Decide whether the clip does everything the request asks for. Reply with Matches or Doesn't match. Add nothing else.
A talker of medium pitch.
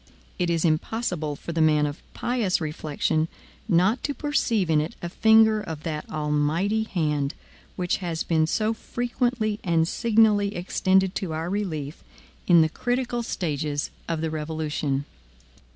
Matches